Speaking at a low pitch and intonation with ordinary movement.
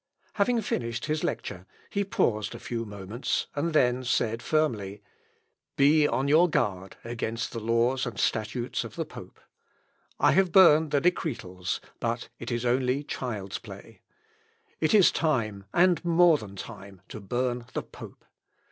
No: low, 120 Hz; wide, 6.1 semitones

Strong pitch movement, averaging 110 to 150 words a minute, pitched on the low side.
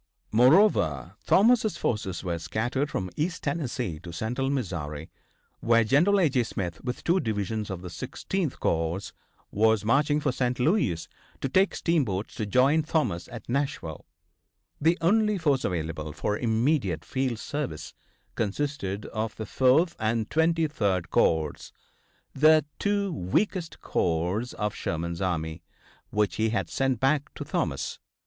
Yes: wide, 8.4 semitones; average, 140 wpm; low, 115 Hz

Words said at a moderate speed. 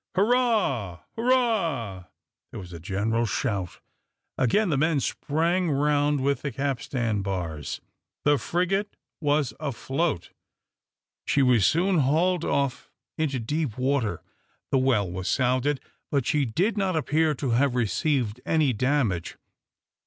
No: slow, 125 wpm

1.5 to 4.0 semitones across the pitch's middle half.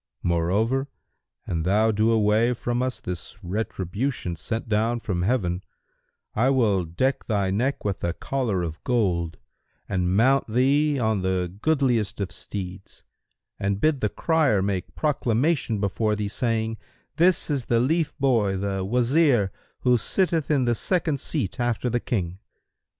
No: average, 5.2 semitones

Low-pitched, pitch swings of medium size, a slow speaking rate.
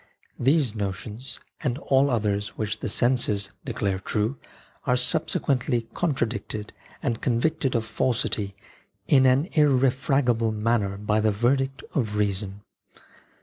Yes: low, 115 Hz; average, 4.1 semitones; slow, 125 wpm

